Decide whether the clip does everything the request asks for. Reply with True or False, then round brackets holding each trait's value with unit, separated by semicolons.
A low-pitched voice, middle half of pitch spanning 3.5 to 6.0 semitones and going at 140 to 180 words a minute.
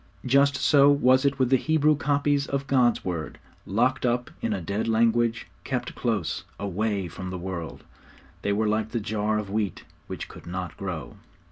True (115 Hz; 4.7 semitones; 175 wpm)